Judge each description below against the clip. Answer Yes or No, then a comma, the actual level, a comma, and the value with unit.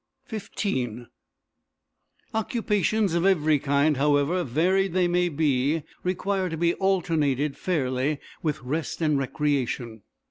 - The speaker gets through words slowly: Yes, slow, 110 wpm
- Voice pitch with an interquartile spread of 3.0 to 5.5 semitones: Yes, average, 4.5 semitones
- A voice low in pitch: No, medium, 155 Hz